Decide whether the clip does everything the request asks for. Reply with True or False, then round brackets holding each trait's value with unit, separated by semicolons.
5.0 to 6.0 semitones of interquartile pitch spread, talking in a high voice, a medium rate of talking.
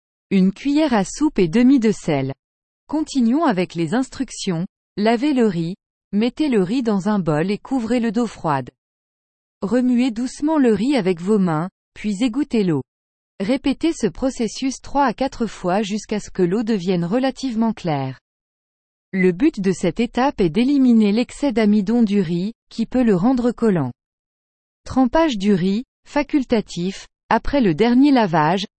True (5.6 semitones; 220 Hz; 155 wpm)